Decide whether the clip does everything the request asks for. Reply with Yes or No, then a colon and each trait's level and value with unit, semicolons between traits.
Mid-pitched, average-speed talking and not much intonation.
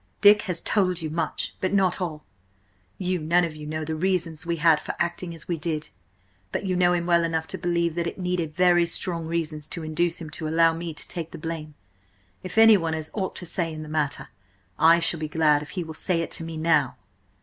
No: medium, 165 Hz; fast, 225 wpm; narrow, 2.0 semitones